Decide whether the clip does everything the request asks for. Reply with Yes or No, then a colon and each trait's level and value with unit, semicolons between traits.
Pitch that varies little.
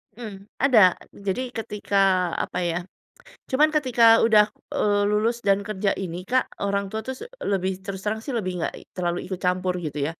No: average, 3.2 semitones